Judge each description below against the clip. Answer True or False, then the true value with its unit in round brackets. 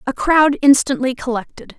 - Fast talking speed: False (135 wpm)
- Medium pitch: False (265 Hz)